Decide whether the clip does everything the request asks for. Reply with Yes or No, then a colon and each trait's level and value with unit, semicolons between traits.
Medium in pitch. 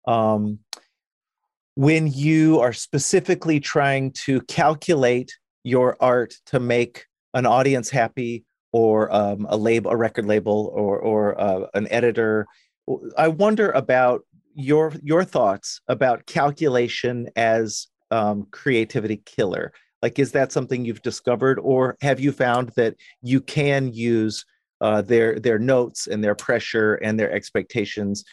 No: low, 120 Hz